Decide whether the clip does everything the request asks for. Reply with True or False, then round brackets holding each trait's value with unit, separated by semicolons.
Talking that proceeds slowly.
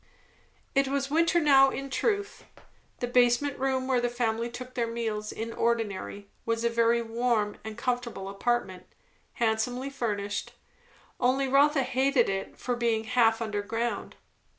False (145 wpm)